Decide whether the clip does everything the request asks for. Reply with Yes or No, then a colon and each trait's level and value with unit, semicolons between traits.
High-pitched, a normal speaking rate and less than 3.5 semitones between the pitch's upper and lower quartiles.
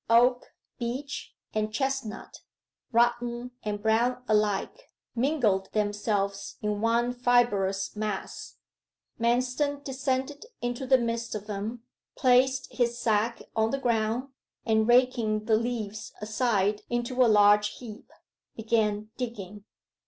No: high, 230 Hz; slow, 115 wpm; average, 2.8 semitones